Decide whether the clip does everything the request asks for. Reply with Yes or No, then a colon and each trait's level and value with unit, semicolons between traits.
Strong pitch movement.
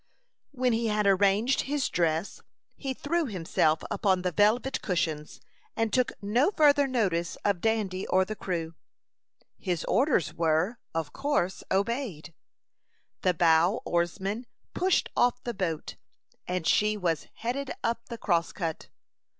Yes: wide, 5.9 semitones